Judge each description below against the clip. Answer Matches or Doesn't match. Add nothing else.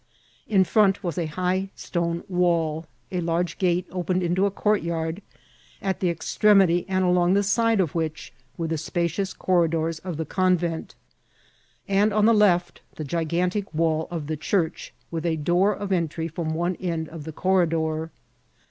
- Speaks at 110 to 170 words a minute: Matches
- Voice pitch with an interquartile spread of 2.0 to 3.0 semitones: Matches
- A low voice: Doesn't match